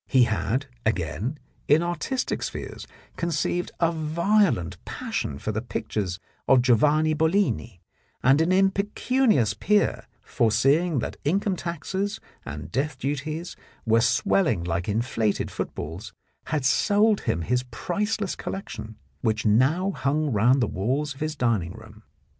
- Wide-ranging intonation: Yes, wide, 7.9 semitones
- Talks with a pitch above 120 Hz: Yes, medium, 140 Hz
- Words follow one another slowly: Yes, slow, 130 wpm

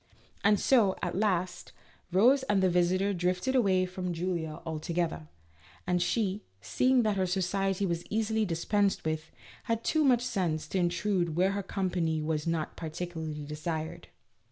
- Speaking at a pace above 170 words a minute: No, average, 155 wpm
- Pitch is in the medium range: Yes, medium, 180 Hz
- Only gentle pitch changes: No, average, 3.3 semitones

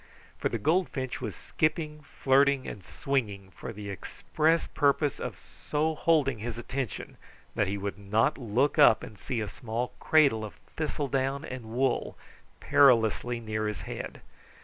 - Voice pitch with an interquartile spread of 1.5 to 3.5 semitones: No, average, 4.8 semitones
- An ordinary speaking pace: Yes, average, 150 wpm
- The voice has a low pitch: Yes, low, 130 Hz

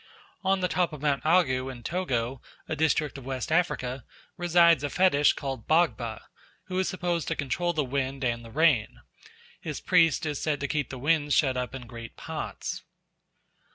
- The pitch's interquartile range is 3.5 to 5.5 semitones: Yes, average, 4.6 semitones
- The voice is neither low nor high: Yes, medium, 145 Hz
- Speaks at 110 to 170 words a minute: No, average, 180 wpm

